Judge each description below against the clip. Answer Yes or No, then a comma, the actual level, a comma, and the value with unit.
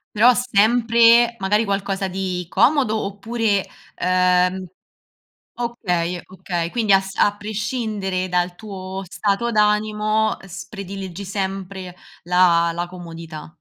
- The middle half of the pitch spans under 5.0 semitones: Yes, average, 2.9 semitones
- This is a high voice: Yes, high, 195 Hz